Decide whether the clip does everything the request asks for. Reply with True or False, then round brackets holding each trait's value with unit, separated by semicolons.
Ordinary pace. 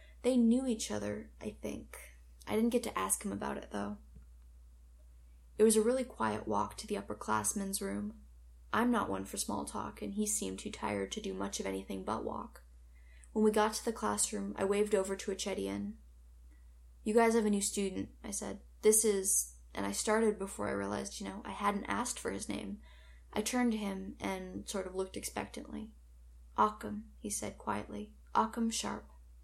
True (190 wpm)